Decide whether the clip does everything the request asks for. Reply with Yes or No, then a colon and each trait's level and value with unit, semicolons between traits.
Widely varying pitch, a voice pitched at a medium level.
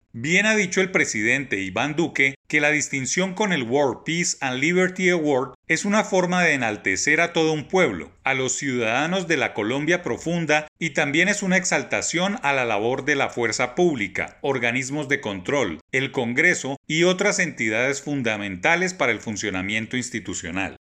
Yes: wide, 6.2 semitones; medium, 145 Hz